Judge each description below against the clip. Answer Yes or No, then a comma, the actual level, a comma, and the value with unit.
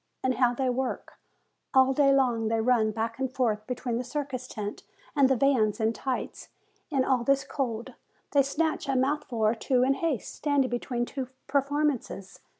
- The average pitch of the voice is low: No, very high, 255 Hz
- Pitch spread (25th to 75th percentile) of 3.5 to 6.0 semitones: No, average, 2.8 semitones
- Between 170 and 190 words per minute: Yes, average, 175 wpm